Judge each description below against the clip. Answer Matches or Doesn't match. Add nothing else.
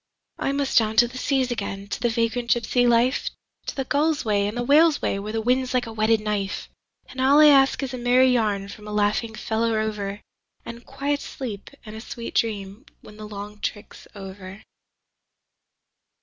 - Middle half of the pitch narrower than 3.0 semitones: Doesn't match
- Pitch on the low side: Doesn't match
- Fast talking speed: Doesn't match